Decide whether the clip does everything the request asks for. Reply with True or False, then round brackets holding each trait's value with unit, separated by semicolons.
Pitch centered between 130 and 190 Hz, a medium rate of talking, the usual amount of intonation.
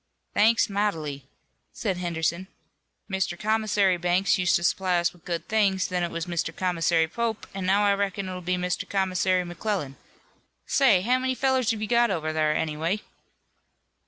True (185 Hz; 165 wpm; 3.2 semitones)